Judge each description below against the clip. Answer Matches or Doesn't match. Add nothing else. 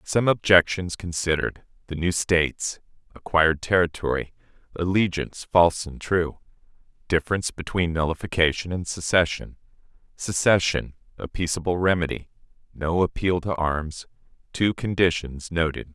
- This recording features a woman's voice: Doesn't match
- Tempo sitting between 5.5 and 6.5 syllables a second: Doesn't match